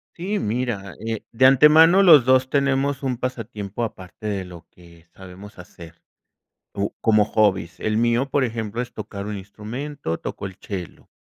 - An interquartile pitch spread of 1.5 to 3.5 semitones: No, average, 5.0 semitones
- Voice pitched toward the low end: Yes, low, 110 Hz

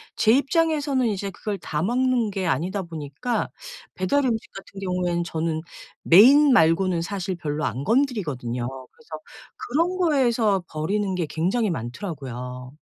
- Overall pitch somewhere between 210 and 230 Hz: No, high, 190 Hz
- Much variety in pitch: Yes, wide, 7.2 semitones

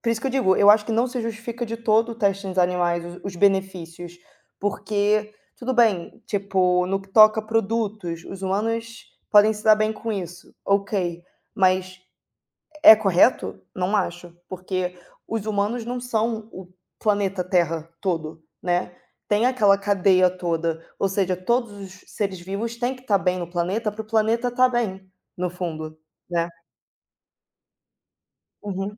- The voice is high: Yes, high, 200 Hz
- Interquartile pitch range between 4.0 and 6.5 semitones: No, average, 3.3 semitones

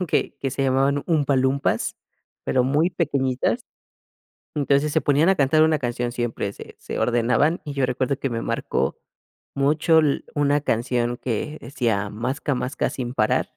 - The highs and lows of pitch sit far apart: No, average, 3.2 semitones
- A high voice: No, low, 135 Hz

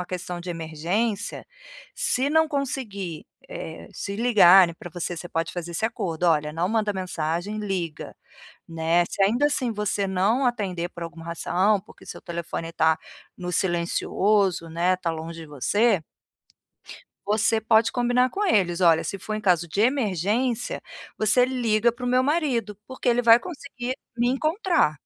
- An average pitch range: No, wide, 5.8 semitones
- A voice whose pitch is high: Yes, high, 200 Hz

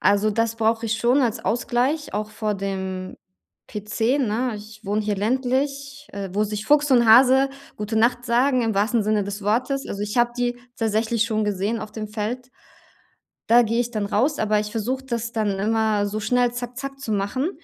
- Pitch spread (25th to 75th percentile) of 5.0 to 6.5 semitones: No, average, 2.9 semitones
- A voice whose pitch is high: Yes, high, 225 Hz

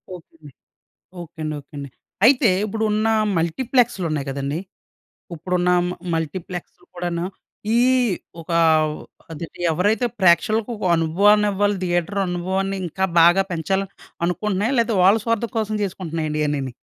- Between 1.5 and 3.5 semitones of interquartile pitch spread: No, average, 4.2 semitones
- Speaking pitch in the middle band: Yes, medium, 180 Hz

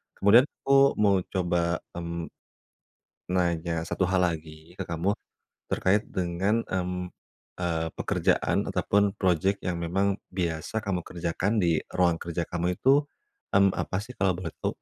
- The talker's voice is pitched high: No, very low, 90 Hz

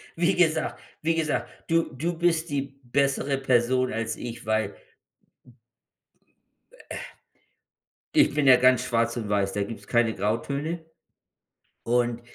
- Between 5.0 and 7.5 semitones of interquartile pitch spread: Yes, average, 5.3 semitones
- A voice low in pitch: Yes, low, 130 Hz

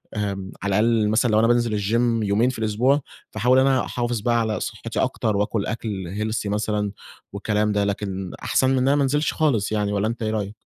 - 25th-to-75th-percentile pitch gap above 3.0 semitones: No, narrow, 2.6 semitones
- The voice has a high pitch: No, low, 110 Hz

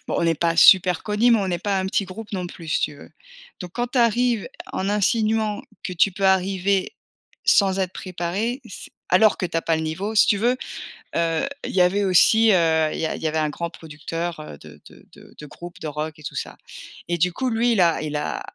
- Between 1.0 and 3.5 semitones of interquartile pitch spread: No, average, 4.1 semitones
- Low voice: No, medium, 185 Hz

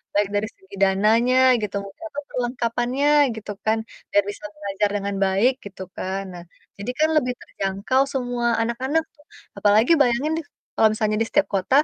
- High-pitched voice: Yes, high, 220 Hz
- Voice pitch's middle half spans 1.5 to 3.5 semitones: No, average, 3.9 semitones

